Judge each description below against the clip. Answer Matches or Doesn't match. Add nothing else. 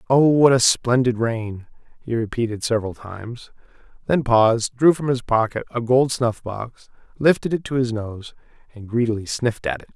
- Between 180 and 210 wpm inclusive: Doesn't match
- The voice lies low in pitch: Matches